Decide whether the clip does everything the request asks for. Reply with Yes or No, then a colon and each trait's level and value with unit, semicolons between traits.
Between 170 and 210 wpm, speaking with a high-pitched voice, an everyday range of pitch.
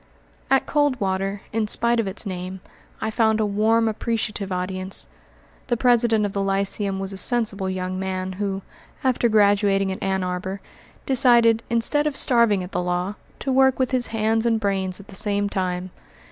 Yes: average, 175 wpm; high, 205 Hz; average, 3.2 semitones